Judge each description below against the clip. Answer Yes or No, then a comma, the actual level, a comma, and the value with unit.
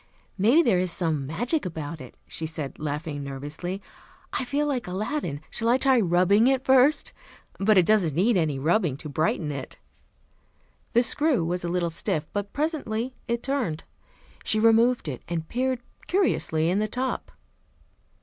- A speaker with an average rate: Yes, average, 160 wpm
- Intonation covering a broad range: Yes, wide, 7.6 semitones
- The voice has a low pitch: No, high, 190 Hz